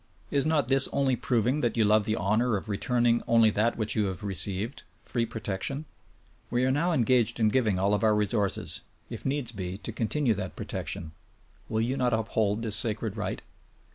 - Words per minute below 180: No, average, 195 wpm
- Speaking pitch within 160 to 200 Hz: No, low, 110 Hz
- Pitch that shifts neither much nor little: Yes, average, 3.2 semitones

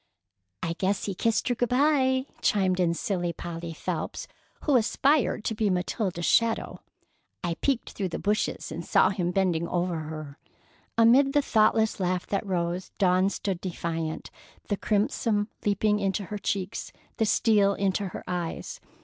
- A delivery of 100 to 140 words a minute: No, average, 155 wpm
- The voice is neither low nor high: No, high, 195 Hz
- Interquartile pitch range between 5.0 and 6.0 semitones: No, average, 3.8 semitones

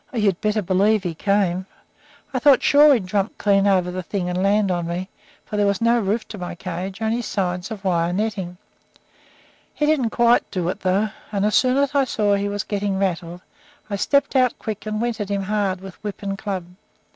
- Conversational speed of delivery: No, fast, 215 wpm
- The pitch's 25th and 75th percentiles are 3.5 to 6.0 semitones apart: No, average, 2.9 semitones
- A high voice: Yes, high, 200 Hz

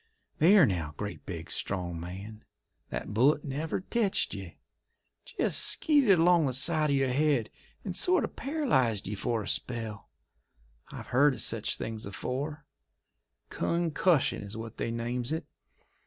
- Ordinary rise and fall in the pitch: No, wide, 7.1 semitones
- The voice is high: No, low, 125 Hz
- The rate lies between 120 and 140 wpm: No, average, 150 wpm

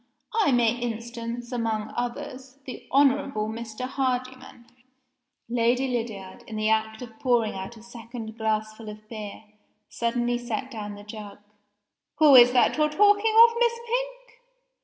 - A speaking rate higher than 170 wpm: No, average, 145 wpm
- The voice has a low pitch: No, high, 240 Hz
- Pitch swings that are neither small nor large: Yes, average, 3.1 semitones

